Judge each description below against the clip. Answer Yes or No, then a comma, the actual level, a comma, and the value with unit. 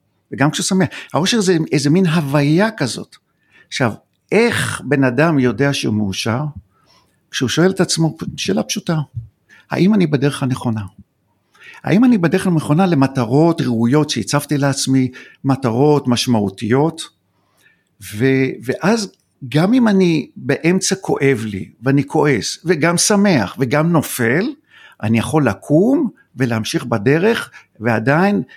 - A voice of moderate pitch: Yes, medium, 145 Hz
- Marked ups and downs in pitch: Yes, wide, 5.7 semitones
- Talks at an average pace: Yes, average, 120 wpm